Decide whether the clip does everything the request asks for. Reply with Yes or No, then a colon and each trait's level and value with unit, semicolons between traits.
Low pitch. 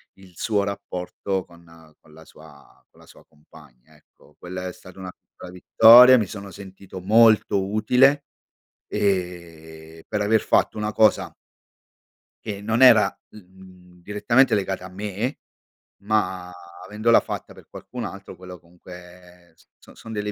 Yes: very low, 95 Hz